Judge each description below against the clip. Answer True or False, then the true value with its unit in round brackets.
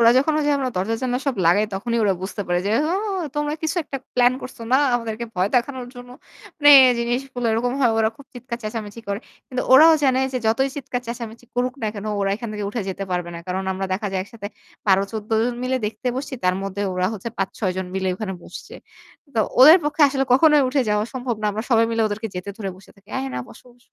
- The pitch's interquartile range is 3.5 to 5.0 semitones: True (4.0 semitones)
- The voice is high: True (230 Hz)